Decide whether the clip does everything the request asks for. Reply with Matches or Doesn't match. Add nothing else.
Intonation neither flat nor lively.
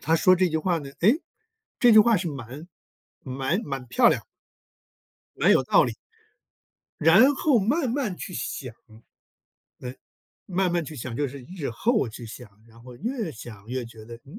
Doesn't match